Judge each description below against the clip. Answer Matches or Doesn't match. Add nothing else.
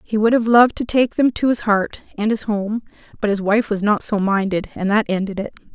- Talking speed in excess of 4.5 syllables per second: Matches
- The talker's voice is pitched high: Matches